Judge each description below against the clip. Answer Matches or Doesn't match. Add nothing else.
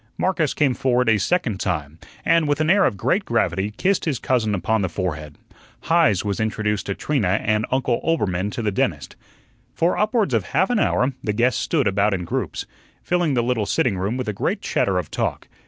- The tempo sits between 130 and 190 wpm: Doesn't match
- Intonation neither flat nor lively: Doesn't match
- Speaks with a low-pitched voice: Matches